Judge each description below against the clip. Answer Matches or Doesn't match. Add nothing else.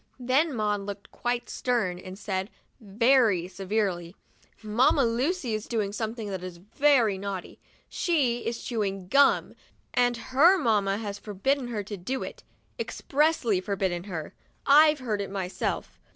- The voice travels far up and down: Doesn't match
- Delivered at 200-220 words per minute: Doesn't match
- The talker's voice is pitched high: Matches